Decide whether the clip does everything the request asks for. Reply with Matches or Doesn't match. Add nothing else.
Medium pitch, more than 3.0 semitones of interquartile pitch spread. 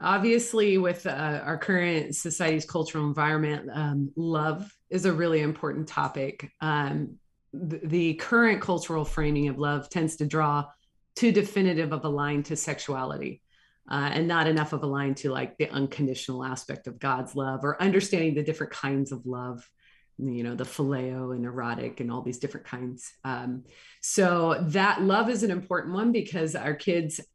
Matches